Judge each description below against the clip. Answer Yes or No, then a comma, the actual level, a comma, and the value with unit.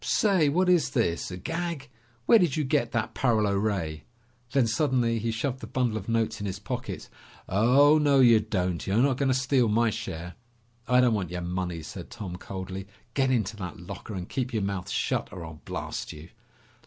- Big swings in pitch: Yes, wide, 5.8 semitones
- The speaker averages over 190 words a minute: Yes, average, 200 wpm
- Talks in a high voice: No, low, 110 Hz